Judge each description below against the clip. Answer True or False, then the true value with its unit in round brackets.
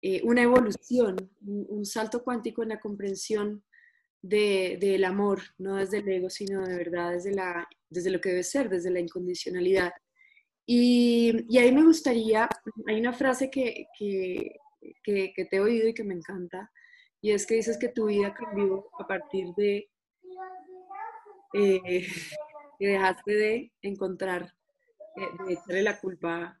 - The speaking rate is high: False (160 wpm)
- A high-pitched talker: True (205 Hz)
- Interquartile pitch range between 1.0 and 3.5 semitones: False (4.4 semitones)